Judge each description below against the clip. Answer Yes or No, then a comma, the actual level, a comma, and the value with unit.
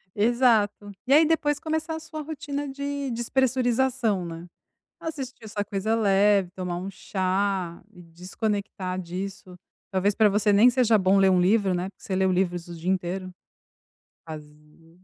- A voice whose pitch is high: Yes, high, 200 Hz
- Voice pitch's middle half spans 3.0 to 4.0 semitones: No, average, 5.2 semitones